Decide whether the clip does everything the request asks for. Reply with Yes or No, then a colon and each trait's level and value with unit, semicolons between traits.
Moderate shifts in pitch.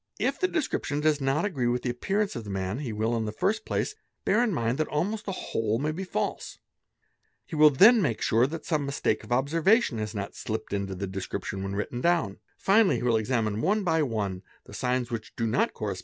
No: wide, 7.4 semitones